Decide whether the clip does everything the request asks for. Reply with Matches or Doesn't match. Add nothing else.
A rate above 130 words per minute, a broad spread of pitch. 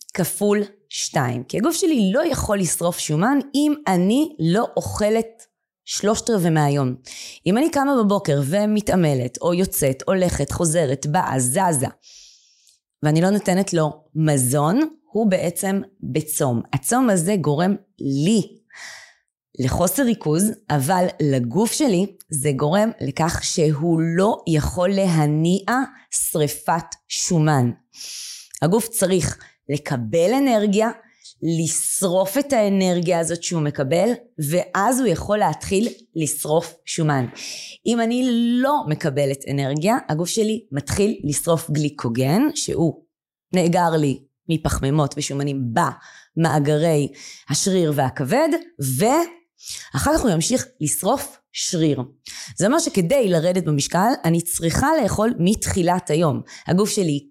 Doesn't match